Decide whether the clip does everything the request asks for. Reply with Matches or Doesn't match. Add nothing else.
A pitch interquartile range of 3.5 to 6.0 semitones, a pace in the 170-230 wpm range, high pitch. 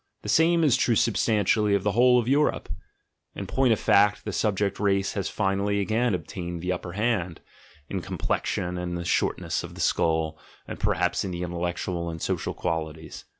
Doesn't match